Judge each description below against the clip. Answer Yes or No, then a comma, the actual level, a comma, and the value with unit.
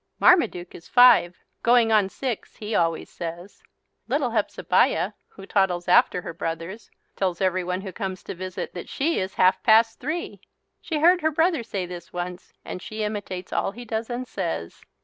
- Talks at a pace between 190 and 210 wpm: No, average, 170 wpm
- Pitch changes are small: No, average, 4.8 semitones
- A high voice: Yes, high, 195 Hz